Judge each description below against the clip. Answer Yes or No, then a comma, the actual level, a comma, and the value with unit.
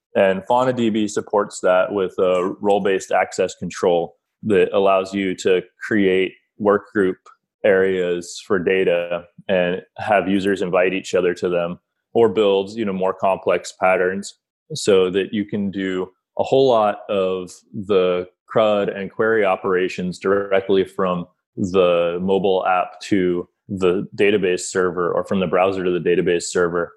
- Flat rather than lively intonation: Yes, narrow, 1.7 semitones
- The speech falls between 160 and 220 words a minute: No, average, 140 wpm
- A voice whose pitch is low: Yes, very low, 95 Hz